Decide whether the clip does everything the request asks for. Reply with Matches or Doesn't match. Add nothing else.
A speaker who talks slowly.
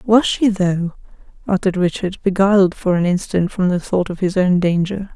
Doesn't match